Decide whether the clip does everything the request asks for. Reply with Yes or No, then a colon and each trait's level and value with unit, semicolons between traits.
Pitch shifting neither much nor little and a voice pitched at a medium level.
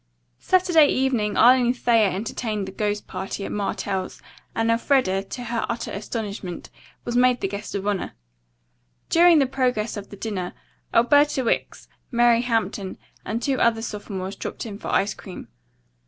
No: average, 3.6 semitones; high, 225 Hz